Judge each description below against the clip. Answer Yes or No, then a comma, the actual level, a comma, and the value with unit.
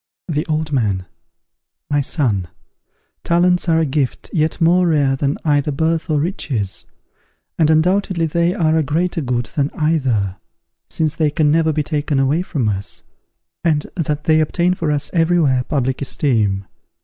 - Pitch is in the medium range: Yes, medium, 150 Hz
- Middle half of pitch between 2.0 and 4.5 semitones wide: Yes, average, 3.3 semitones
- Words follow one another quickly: No, average, 160 wpm